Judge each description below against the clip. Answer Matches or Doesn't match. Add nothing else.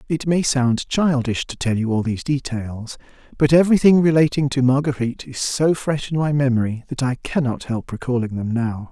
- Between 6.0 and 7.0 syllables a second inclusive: Doesn't match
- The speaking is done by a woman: Doesn't match